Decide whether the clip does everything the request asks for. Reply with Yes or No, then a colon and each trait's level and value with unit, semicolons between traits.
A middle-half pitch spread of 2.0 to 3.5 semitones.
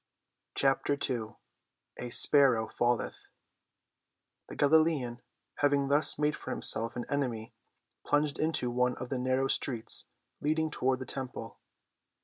Yes: average, 2.9 semitones